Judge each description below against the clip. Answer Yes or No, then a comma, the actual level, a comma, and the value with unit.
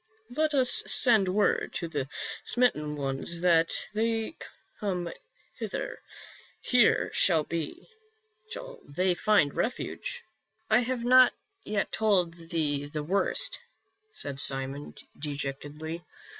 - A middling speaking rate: No, slow, 105 wpm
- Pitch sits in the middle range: Yes, medium, 175 Hz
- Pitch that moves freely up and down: Yes, wide, 7.1 semitones